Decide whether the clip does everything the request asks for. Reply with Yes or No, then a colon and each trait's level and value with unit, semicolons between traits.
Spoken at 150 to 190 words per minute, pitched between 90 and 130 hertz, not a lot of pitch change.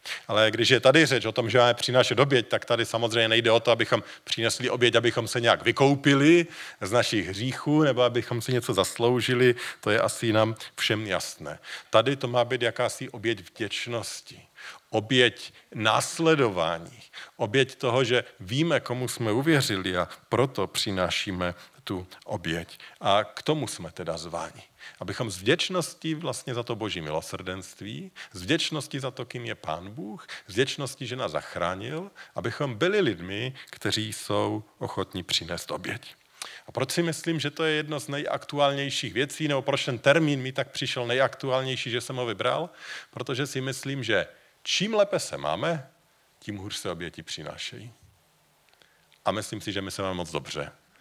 No: average, 165 wpm; low, 125 Hz; average, 4.1 semitones